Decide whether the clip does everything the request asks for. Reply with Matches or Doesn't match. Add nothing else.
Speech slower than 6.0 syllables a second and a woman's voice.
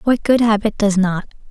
Matches